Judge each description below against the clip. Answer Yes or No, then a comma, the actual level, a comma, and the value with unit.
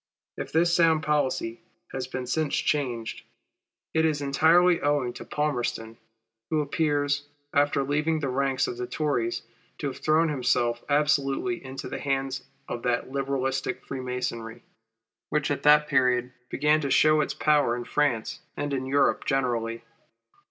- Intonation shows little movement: No, average, 3.0 semitones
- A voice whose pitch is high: No, medium, 140 Hz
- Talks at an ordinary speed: Yes, average, 145 wpm